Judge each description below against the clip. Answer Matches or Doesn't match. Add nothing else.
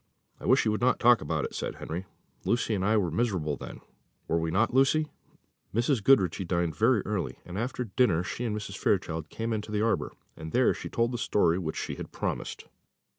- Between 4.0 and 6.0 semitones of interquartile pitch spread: Matches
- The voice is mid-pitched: Doesn't match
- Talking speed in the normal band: Doesn't match